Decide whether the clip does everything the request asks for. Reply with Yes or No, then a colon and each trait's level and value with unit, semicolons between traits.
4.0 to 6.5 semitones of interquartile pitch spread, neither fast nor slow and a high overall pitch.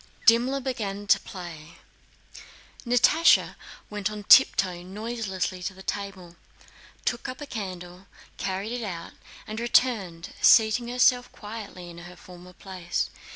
No: average, 4.7 semitones; slow, 125 wpm; high, 200 Hz